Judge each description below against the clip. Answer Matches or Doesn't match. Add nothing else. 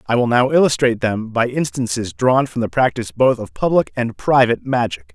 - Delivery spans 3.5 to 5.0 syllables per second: Doesn't match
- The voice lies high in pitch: Doesn't match